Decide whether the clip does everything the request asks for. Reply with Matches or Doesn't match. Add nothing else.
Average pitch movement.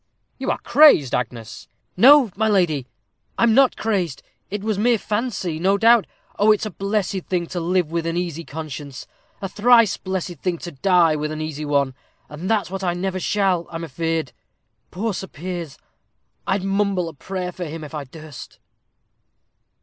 Matches